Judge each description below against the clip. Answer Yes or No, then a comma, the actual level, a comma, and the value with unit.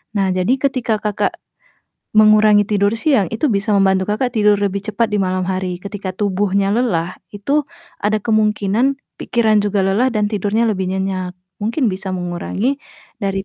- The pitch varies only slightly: Yes, narrow, 2.2 semitones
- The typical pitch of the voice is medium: No, high, 205 Hz